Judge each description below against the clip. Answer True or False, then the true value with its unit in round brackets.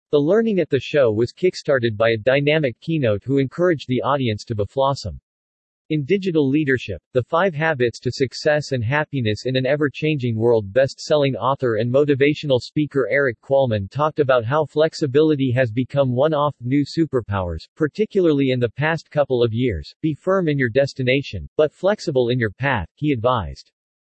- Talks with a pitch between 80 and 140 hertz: True (135 Hz)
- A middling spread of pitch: True (4.0 semitones)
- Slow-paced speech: False (175 wpm)